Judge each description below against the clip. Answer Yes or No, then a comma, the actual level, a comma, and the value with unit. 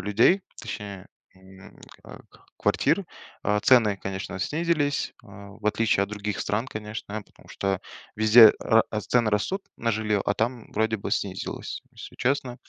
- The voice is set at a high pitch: No, low, 105 Hz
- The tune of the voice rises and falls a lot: No, average, 2.8 semitones